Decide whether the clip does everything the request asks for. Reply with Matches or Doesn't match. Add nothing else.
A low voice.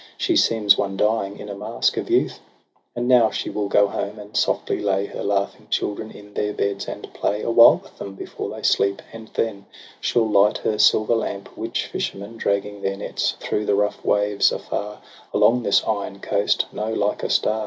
Matches